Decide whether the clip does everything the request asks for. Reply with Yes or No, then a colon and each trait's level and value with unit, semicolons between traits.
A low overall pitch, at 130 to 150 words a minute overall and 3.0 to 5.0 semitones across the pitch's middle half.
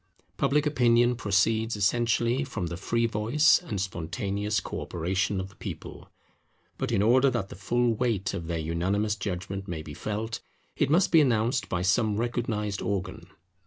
No: low, 105 Hz; average, 160 wpm; average, 3.8 semitones